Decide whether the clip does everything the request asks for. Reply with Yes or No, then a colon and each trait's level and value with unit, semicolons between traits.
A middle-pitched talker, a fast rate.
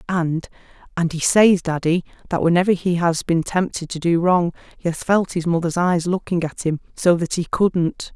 No: medium, 170 Hz; average, 190 wpm